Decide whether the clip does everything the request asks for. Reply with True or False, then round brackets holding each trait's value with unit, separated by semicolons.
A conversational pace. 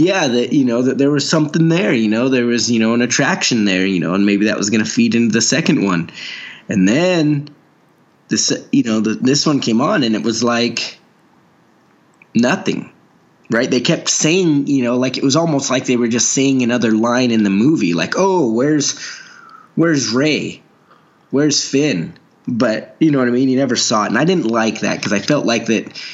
False (215 wpm)